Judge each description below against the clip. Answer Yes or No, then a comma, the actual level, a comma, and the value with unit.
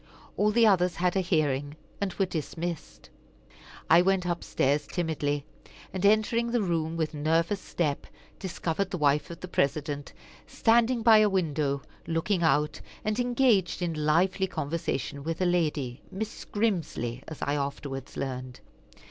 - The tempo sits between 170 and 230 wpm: No, average, 150 wpm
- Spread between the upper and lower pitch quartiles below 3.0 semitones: No, average, 4.7 semitones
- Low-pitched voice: No, medium, 170 Hz